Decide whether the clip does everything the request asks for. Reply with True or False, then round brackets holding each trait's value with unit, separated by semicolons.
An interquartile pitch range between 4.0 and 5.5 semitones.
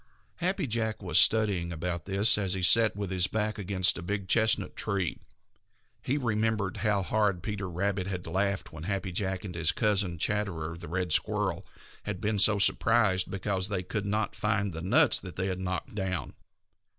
False (2.6 semitones)